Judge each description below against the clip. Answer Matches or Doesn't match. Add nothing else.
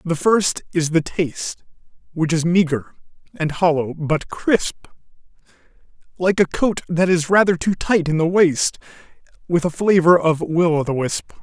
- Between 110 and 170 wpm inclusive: Matches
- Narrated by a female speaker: Doesn't match